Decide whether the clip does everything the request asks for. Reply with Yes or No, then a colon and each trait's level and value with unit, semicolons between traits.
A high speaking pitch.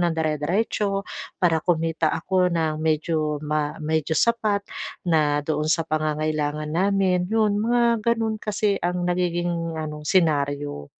No: medium, 165 Hz